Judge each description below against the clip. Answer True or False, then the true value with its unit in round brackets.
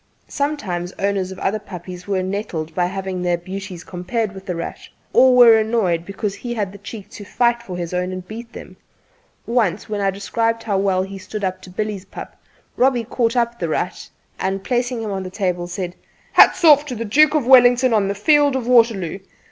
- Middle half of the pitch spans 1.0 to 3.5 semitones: False (4.2 semitones)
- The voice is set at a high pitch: True (200 Hz)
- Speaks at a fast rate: True (210 wpm)